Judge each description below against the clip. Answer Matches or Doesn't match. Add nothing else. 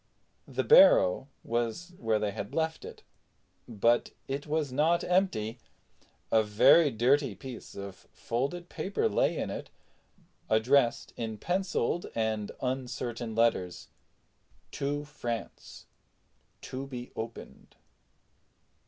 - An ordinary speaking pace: Doesn't match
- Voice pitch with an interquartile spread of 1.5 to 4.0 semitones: Doesn't match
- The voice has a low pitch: Matches